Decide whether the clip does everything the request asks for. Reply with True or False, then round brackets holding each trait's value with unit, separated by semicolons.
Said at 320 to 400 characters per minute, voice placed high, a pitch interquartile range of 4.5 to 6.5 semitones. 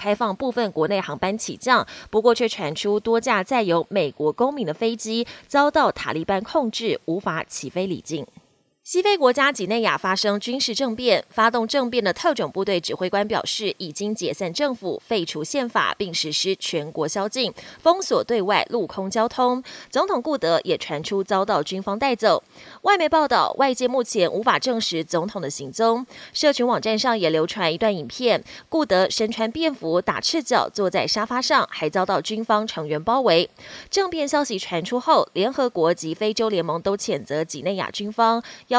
False (275 characters per minute; 220 Hz; 5.1 semitones)